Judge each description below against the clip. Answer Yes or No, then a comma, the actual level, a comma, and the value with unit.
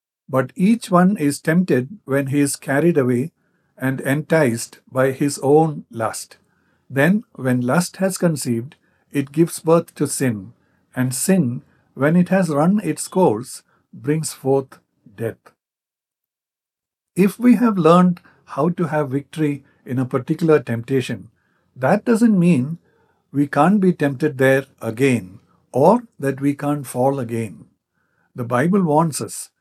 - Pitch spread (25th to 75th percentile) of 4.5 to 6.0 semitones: Yes, average, 5.0 semitones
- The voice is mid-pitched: Yes, medium, 145 Hz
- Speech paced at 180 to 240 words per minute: No, average, 140 wpm